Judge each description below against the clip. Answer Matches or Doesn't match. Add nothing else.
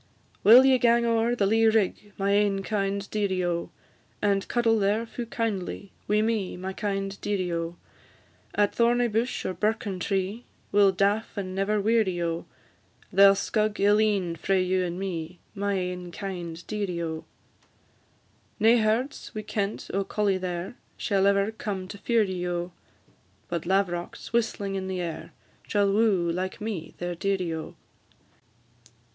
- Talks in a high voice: Matches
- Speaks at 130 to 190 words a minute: Matches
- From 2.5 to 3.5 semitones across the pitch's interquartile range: Matches